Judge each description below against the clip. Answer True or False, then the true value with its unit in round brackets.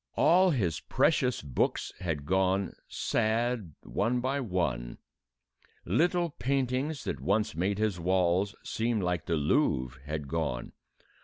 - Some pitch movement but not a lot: False (7.1 semitones)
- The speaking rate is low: True (125 wpm)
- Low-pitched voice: True (95 Hz)